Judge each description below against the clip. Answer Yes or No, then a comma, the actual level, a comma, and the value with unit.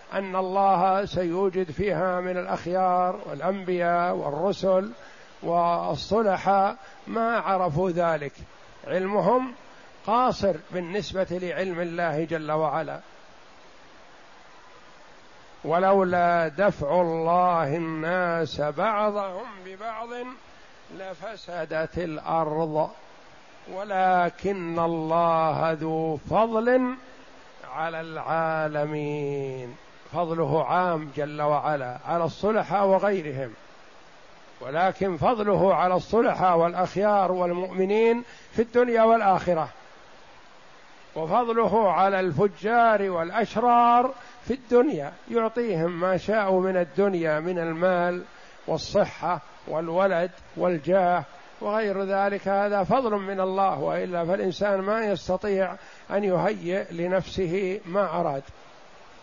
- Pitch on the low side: No, medium, 185 Hz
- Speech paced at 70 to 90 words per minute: Yes, average, 80 wpm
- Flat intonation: No, average, 3.1 semitones